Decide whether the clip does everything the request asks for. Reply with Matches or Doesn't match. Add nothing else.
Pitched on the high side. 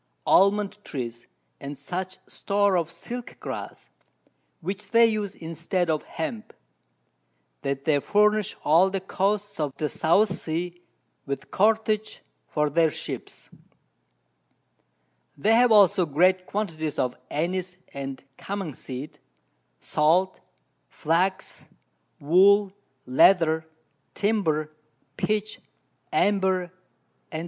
Doesn't match